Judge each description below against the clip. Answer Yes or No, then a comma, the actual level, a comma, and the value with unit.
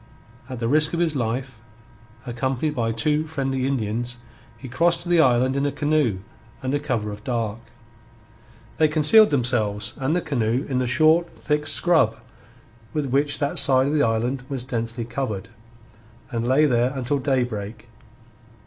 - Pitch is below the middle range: Yes, low, 130 Hz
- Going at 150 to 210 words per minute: Yes, average, 160 wpm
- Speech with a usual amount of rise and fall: Yes, average, 4.0 semitones